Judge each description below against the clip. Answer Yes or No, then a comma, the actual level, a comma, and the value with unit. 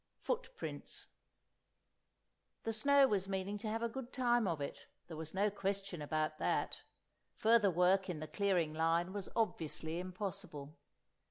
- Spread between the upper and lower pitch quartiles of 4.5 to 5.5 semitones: Yes, average, 4.8 semitones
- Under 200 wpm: Yes, average, 150 wpm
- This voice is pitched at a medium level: No, high, 195 Hz